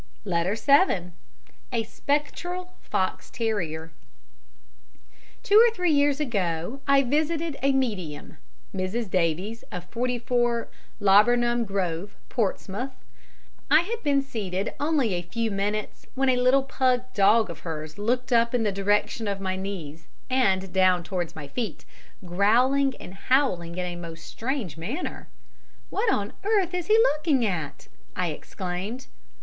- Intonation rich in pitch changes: Yes, wide, 6.6 semitones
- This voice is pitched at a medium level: No, high, 225 Hz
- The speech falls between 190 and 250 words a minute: No, slow, 135 wpm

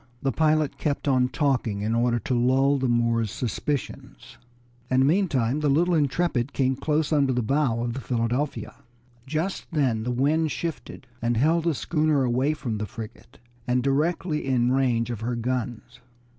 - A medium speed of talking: Yes, average, 170 wpm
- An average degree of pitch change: Yes, average, 4.0 semitones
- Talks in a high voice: No, low, 130 Hz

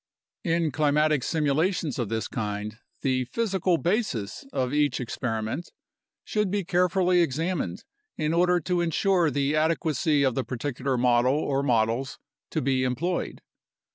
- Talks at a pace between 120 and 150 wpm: Yes, average, 140 wpm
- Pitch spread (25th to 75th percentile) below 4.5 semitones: No, average, 5.3 semitones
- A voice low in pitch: No, medium, 145 Hz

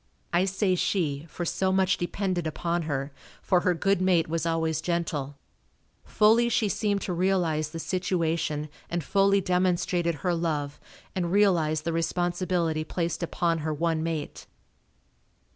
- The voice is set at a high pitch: No, medium, 170 Hz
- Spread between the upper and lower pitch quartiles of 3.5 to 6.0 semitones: No, narrow, 2.6 semitones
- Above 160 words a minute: No, average, 145 wpm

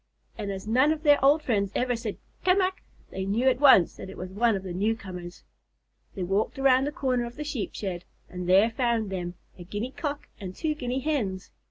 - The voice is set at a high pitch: Yes, high, 225 Hz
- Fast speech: Yes, fast, 215 wpm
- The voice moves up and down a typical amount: No, wide, 5.9 semitones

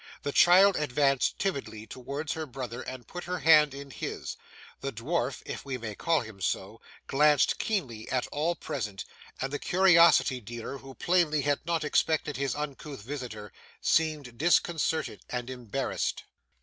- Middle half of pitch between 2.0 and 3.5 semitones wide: No, average, 4.4 semitones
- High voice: No, medium, 140 Hz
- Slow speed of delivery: No, average, 150 wpm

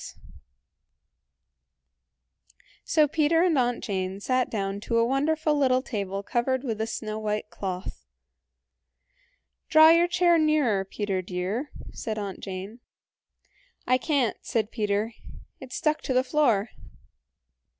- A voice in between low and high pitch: No, high, 235 Hz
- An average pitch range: No, wide, 6.3 semitones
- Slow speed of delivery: Yes, slow, 120 wpm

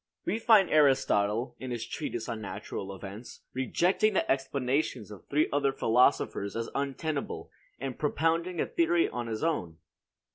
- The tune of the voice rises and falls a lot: Yes, wide, 5.7 semitones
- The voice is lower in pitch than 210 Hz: Yes, low, 135 Hz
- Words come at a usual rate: Yes, average, 145 wpm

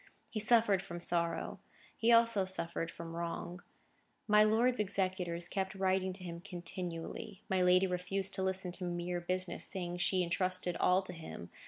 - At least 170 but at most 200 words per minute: No, average, 160 wpm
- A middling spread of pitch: No, narrow, 1.9 semitones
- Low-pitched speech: No, medium, 185 Hz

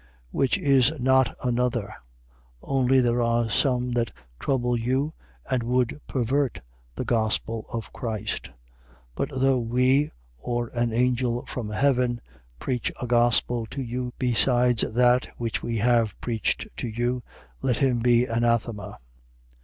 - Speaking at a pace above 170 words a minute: No, average, 140 wpm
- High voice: No, low, 120 Hz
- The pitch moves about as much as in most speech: No, narrow, 1.5 semitones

